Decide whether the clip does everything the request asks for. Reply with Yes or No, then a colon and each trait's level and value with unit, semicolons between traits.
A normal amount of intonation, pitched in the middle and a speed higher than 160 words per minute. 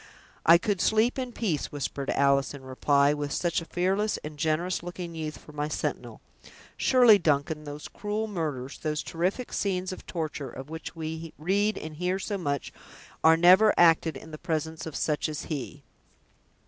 Yes: average, 3.8 semitones; medium, 160 Hz; average, 175 wpm